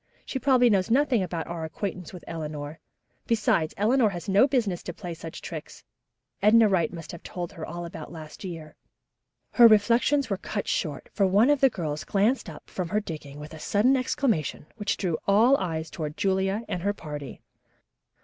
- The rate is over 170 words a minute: Yes, average, 185 wpm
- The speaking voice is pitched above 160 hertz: Yes, high, 190 Hz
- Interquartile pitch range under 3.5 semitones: No, wide, 5.4 semitones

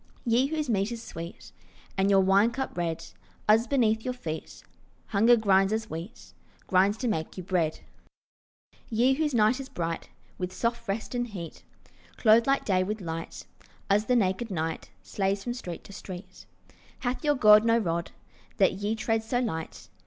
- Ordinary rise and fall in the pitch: Yes, average, 4.2 semitones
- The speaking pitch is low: No, high, 210 Hz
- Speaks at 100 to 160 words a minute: No, average, 170 wpm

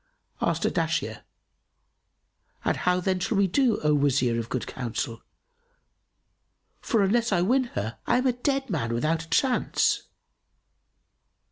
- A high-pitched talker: No, medium, 180 Hz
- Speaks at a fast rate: No, slow, 135 wpm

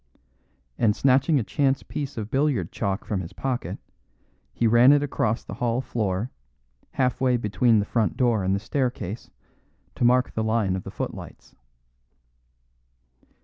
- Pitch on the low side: Yes, low, 120 Hz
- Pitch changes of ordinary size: Yes, average, 3.7 semitones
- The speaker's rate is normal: Yes, average, 150 wpm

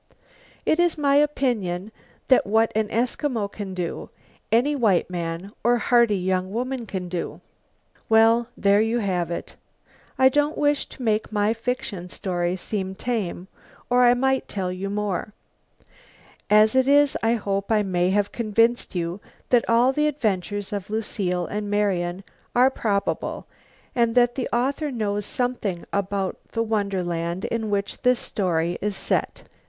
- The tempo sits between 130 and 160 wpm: Yes, average, 150 wpm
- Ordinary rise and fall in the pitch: Yes, average, 4.2 semitones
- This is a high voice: Yes, high, 210 Hz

